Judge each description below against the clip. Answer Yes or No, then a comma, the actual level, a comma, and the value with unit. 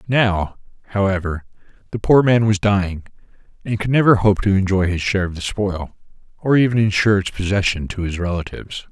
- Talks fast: No, average, 175 wpm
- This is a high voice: No, low, 100 Hz